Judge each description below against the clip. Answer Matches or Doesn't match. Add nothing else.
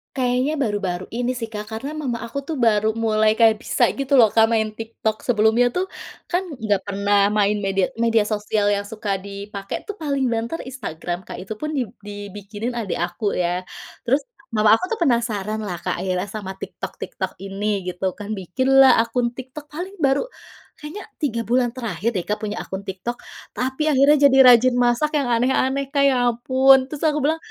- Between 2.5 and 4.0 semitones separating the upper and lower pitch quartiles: Doesn't match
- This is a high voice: Matches